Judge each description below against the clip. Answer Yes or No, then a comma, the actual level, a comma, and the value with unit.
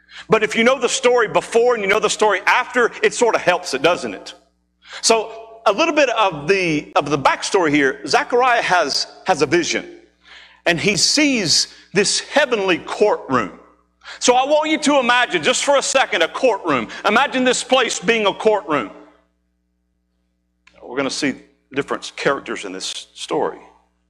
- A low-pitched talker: No, high, 215 Hz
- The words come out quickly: No, average, 170 wpm